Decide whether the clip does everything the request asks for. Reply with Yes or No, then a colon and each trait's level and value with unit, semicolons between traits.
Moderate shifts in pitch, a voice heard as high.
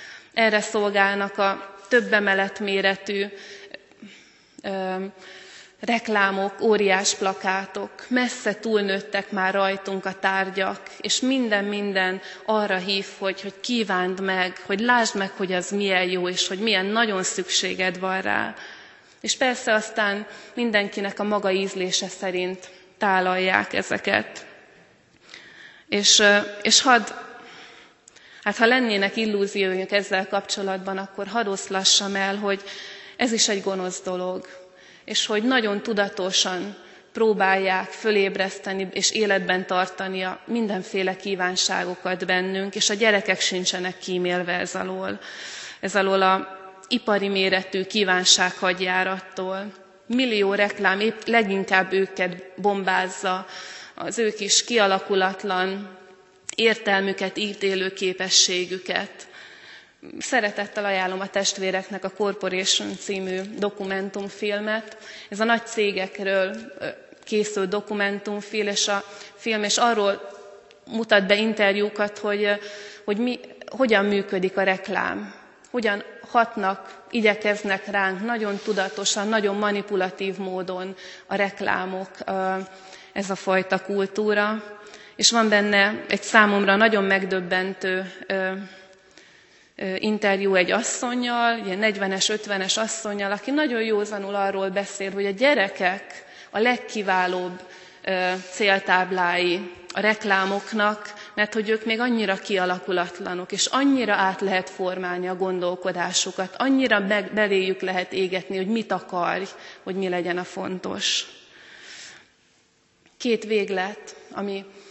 No: narrow, 1.8 semitones; high, 195 Hz